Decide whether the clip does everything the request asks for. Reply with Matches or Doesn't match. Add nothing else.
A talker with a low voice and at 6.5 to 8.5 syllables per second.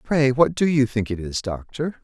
Doesn't match